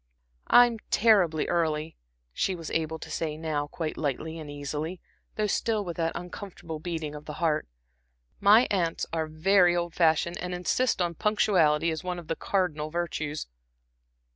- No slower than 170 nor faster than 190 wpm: No, average, 160 wpm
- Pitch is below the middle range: No, medium, 165 Hz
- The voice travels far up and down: No, average, 2.7 semitones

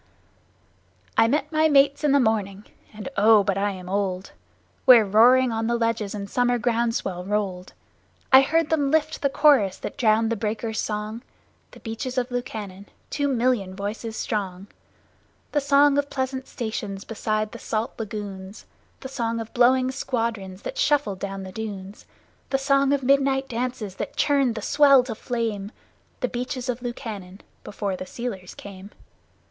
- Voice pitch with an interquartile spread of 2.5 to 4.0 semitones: No, average, 4.4 semitones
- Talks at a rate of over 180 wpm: No, average, 165 wpm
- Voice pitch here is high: Yes, high, 230 Hz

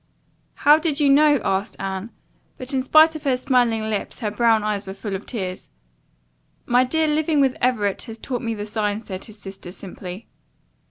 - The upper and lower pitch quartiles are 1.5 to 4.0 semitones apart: No, average, 4.9 semitones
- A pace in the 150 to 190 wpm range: Yes, average, 185 wpm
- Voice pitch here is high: Yes, high, 225 Hz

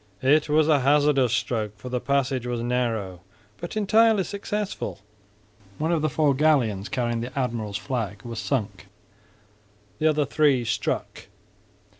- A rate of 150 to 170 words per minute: No, average, 140 wpm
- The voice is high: No, low, 130 Hz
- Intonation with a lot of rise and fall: No, average, 4.7 semitones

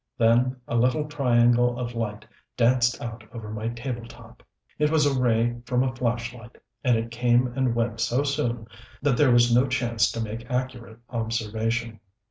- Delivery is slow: No, average, 170 wpm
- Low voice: Yes, low, 120 Hz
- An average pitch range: No, narrow, 1.6 semitones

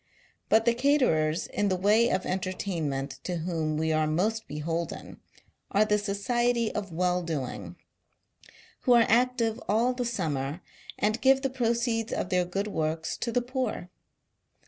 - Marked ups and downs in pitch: Yes, wide, 6.3 semitones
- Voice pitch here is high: Yes, high, 200 Hz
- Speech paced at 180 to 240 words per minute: No, average, 145 wpm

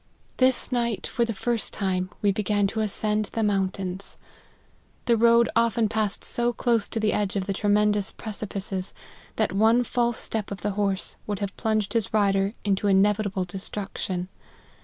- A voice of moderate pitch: No, high, 210 Hz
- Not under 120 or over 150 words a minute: No, average, 165 wpm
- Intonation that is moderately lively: No, narrow, 2.3 semitones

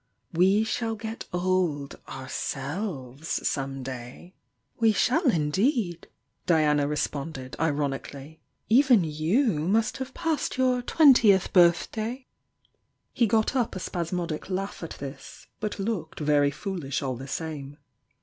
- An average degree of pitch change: No, wide, 7.2 semitones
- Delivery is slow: Yes, slow, 120 wpm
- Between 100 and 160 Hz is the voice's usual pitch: No, medium, 175 Hz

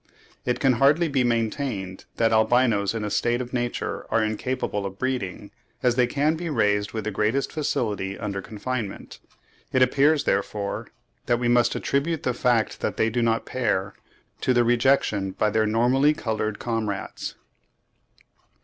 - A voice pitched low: Yes, low, 120 Hz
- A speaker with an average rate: Yes, average, 160 wpm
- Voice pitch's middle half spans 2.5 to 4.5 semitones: Yes, average, 3.3 semitones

